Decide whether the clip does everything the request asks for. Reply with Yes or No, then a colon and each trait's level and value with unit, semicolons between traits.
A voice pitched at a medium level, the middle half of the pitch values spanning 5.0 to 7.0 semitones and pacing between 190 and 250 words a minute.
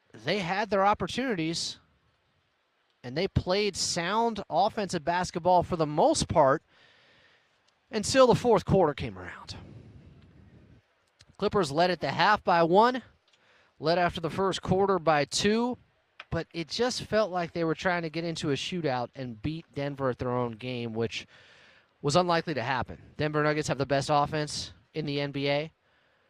No: medium, 165 Hz; average, 5.3 semitones; average, 155 wpm